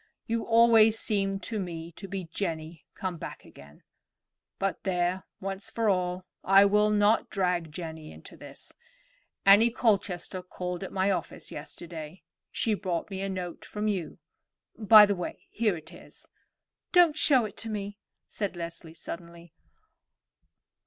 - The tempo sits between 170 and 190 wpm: No, average, 145 wpm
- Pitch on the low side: No, high, 190 Hz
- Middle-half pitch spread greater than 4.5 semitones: No, average, 3.3 semitones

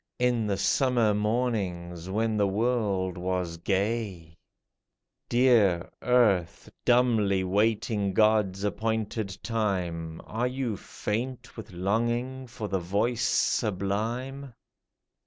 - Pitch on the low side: Yes, low, 105 Hz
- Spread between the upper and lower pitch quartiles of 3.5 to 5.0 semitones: Yes, average, 3.8 semitones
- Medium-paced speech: No, slow, 100 wpm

